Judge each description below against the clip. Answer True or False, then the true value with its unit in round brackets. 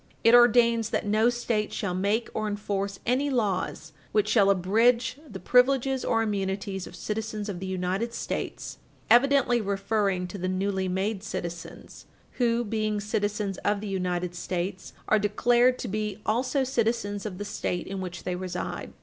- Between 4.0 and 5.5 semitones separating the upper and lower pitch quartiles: False (3.4 semitones)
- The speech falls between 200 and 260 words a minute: False (160 wpm)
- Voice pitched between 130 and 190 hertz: False (210 Hz)